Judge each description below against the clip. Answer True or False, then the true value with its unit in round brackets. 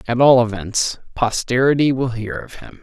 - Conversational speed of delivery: True (170 wpm)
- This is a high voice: False (120 Hz)